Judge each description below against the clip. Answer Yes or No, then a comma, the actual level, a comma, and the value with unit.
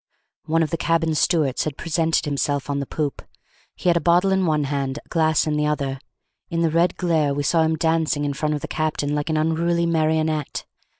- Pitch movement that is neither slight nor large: No, narrow, 2.1 semitones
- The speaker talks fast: Yes, fast, 220 wpm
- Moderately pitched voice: Yes, medium, 155 Hz